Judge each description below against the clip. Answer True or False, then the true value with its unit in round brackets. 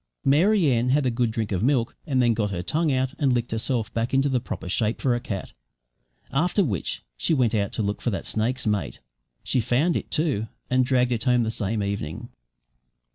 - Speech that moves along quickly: True (215 wpm)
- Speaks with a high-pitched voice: False (120 Hz)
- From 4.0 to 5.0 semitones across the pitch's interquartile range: False (3.5 semitones)